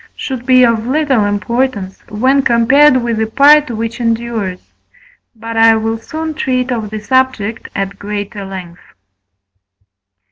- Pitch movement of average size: Yes, average, 3.6 semitones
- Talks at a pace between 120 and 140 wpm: Yes, slow, 135 wpm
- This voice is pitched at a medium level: No, high, 230 Hz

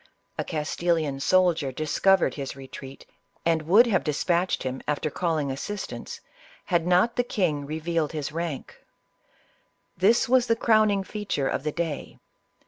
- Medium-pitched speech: Yes, medium, 165 Hz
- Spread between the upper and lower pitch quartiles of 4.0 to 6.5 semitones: Yes, average, 4.5 semitones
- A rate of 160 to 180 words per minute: No, slow, 135 wpm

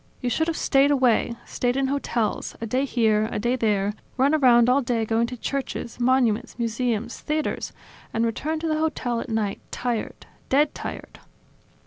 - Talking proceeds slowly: No, average, 170 wpm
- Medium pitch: No, high, 245 Hz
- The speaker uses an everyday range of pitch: Yes, average, 3.1 semitones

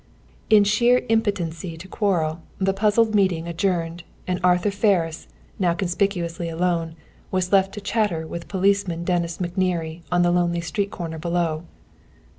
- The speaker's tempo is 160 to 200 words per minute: No, average, 140 wpm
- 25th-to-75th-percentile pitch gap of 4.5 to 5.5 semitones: No, average, 2.9 semitones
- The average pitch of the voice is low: No, medium, 180 Hz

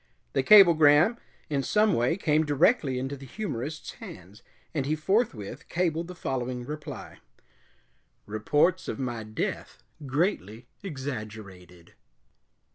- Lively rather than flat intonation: Yes, wide, 6.1 semitones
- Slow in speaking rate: Yes, slow, 115 wpm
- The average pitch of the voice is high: No, medium, 145 Hz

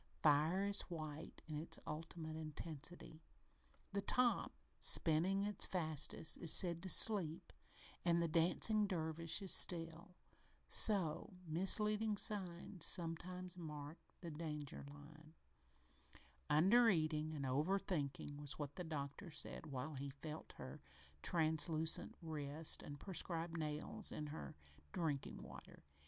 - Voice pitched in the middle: Yes, medium, 160 Hz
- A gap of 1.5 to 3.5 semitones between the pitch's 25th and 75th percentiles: Yes, average, 3.0 semitones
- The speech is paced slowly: Yes, slow, 120 wpm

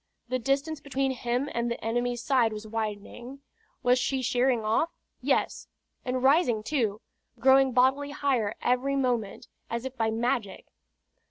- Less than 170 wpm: Yes, average, 145 wpm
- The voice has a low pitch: No, very high, 250 Hz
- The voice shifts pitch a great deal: No, average, 2.9 semitones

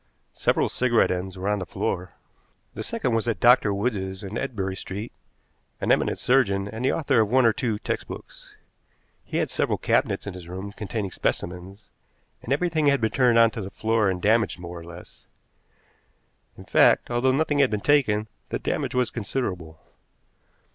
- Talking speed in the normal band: Yes, average, 175 wpm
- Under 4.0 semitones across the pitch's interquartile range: No, average, 4.5 semitones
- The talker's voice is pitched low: Yes, low, 110 Hz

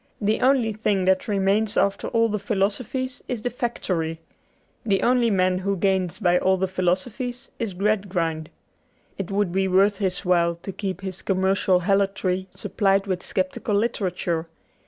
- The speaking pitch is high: Yes, high, 195 Hz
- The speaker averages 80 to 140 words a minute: No, average, 155 wpm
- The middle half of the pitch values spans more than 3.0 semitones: No, narrow, 2.5 semitones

